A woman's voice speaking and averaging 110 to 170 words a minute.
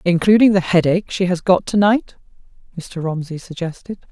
Yes: female; average, 160 wpm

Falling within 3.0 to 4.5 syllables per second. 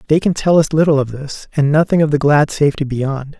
No: 5.8 syllables/s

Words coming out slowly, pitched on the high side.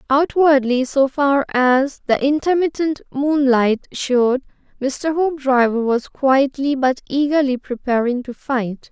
Yes: slow, 115 wpm; very high, 270 Hz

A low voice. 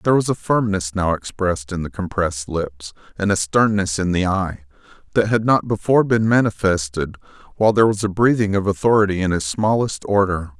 Yes: low, 100 Hz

